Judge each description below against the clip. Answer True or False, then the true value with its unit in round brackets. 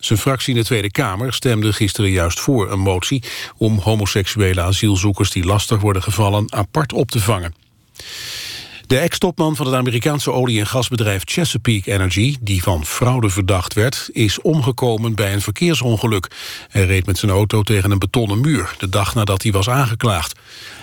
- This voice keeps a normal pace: True (165 wpm)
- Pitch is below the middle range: True (110 Hz)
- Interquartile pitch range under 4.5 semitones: True (3.8 semitones)